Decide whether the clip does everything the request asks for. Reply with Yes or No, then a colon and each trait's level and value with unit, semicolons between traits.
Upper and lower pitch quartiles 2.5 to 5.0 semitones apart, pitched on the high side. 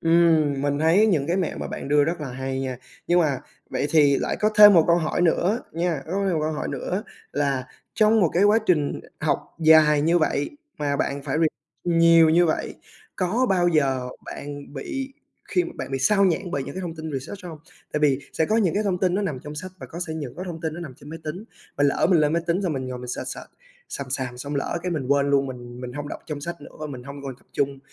No: average, 3.9 semitones; medium, 155 Hz